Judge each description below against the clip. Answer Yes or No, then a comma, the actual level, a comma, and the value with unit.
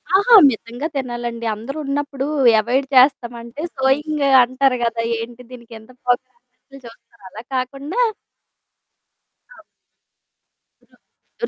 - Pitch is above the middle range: Yes, very high, 255 Hz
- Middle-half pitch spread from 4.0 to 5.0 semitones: No, average, 2.7 semitones